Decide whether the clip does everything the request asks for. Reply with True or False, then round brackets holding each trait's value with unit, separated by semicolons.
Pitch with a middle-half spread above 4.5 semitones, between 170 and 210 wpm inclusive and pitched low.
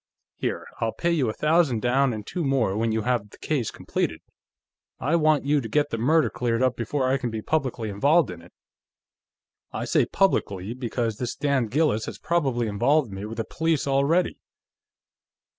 True (5.0 semitones; 185 wpm; 130 Hz)